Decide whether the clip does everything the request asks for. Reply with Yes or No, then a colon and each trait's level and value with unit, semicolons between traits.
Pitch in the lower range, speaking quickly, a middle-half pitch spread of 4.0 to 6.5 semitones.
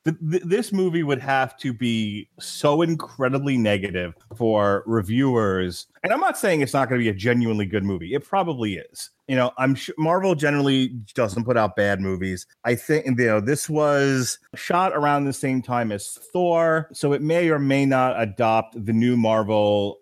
No: low, 130 Hz; average, 185 wpm; average, 5.0 semitones